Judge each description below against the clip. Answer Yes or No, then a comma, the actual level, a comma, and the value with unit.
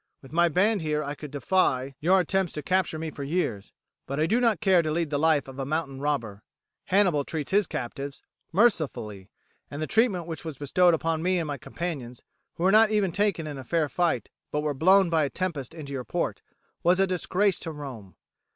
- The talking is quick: Yes, fast, 210 wpm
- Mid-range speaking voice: Yes, medium, 160 Hz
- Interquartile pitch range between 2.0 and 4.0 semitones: No, average, 4.5 semitones